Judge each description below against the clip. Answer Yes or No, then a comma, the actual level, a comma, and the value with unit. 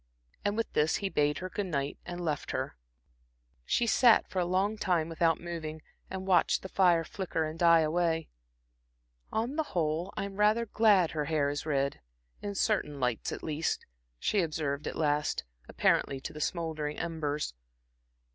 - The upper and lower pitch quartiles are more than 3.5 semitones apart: Yes, average, 4.0 semitones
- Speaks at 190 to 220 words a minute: No, average, 165 wpm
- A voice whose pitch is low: No, medium, 165 Hz